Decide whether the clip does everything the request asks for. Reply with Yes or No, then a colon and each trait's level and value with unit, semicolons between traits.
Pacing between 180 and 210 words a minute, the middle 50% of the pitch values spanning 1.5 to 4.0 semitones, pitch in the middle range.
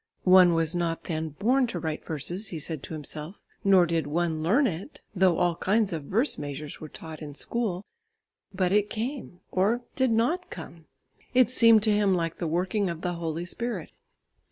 No: average, 185 wpm; average, 4.8 semitones; medium, 180 Hz